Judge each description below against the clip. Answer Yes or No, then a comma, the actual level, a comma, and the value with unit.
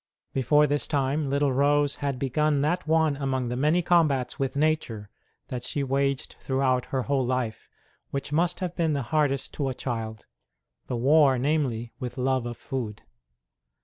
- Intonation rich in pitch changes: No, average, 2.8 semitones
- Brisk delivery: No, average, 165 wpm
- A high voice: No, low, 135 Hz